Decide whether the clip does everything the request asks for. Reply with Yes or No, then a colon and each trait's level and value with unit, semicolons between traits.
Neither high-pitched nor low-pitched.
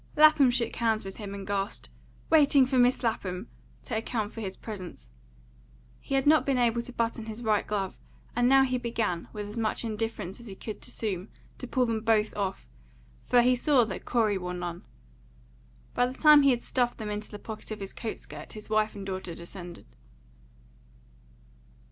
No: high, 220 Hz